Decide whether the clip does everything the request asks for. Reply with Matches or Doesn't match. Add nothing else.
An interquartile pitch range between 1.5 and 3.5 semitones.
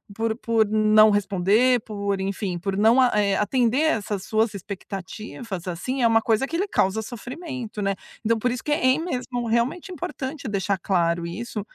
Doesn't match